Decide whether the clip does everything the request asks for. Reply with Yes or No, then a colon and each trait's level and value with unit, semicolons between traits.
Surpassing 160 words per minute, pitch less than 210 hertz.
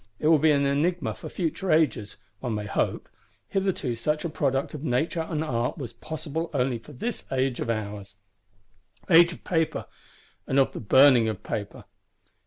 Yes: average, 170 wpm; medium, 140 Hz